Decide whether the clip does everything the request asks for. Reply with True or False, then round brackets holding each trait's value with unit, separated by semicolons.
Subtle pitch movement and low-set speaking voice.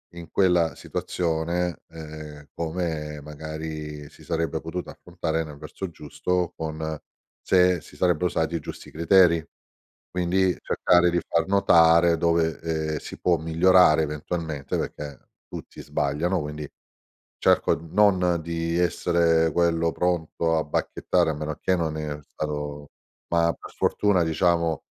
True (2.1 semitones; 80 Hz)